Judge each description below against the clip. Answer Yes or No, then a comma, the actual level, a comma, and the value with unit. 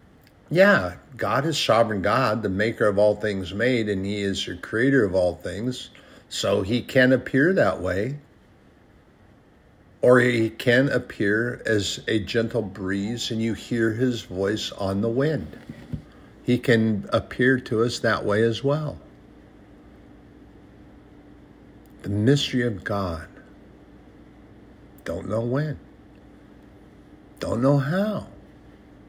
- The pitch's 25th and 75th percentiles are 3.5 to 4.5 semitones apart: Yes, average, 3.9 semitones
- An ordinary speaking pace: No, slow, 125 wpm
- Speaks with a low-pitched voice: Yes, low, 110 Hz